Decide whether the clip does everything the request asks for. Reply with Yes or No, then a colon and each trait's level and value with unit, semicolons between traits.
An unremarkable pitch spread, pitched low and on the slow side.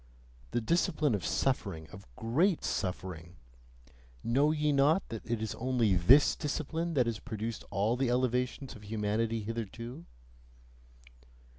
Yes: average, 4.5 semitones; low, 115 Hz; slow, 130 wpm